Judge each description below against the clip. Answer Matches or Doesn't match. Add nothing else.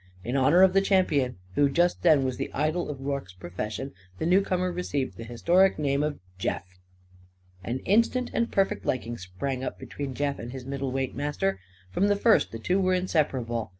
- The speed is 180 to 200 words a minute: Matches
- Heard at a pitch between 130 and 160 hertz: Matches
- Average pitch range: Doesn't match